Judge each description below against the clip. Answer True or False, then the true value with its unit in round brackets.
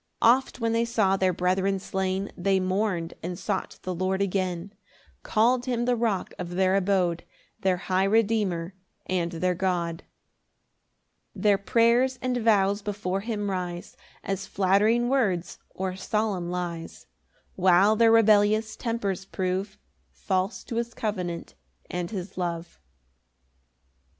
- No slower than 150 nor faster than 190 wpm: False (135 wpm)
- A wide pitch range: False (3.2 semitones)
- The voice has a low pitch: False (195 Hz)